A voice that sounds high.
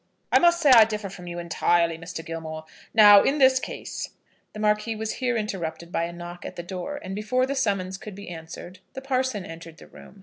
Yes: high, 200 Hz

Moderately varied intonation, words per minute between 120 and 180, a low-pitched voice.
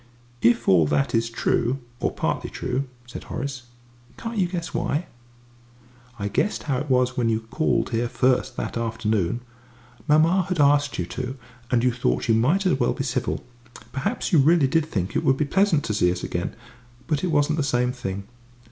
No: average, 4.6 semitones; average, 190 wpm; low, 130 Hz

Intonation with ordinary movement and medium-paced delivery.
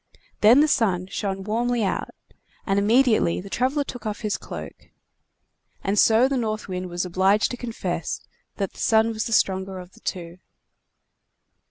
Yes: average, 3.6 semitones; average, 165 wpm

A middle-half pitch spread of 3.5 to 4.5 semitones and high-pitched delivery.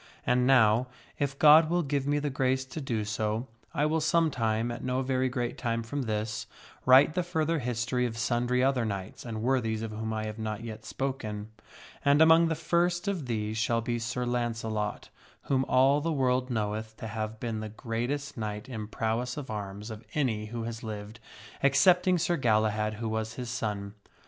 No: average, 3.8 semitones; low, 120 Hz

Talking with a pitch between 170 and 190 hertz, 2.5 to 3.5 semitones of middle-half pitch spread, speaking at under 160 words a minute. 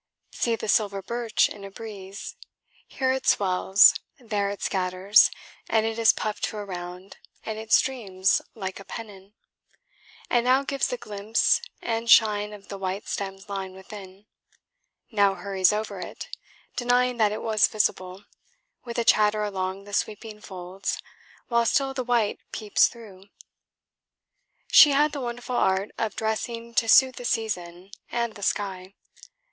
No: high, 210 Hz; average, 3.2 semitones; average, 150 wpm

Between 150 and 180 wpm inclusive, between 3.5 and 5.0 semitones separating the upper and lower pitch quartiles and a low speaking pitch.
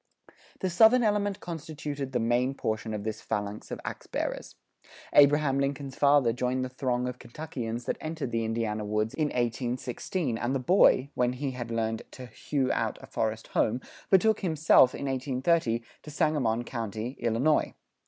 Yes: average, 165 wpm; average, 4.2 semitones; low, 130 Hz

